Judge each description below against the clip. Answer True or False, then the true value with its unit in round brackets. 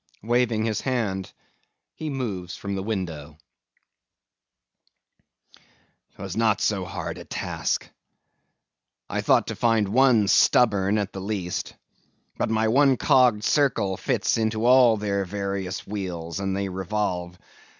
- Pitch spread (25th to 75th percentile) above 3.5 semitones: False (3.2 semitones)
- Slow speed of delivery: True (125 wpm)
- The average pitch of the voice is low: True (105 Hz)